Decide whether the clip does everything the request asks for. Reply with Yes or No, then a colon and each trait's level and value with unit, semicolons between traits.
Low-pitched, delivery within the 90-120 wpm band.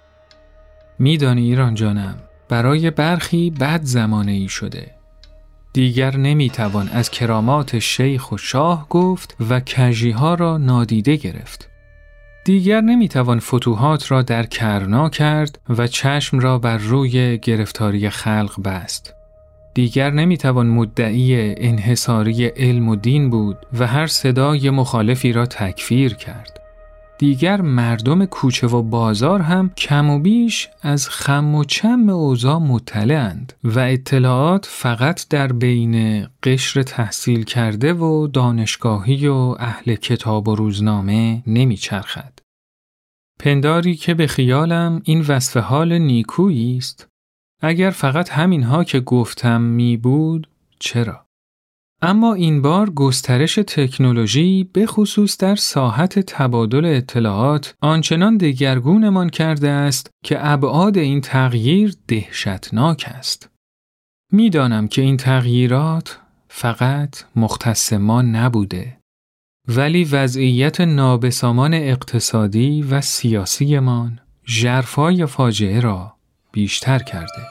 Yes: low, 130 Hz; average, 110 wpm